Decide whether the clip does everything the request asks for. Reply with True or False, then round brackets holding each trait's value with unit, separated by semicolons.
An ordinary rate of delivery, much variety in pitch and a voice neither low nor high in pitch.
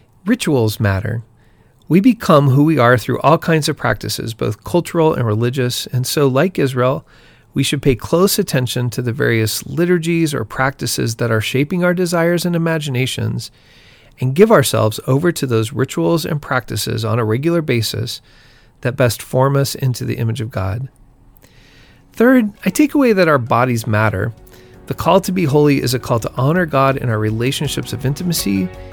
False (175 wpm; 5.8 semitones; 130 Hz)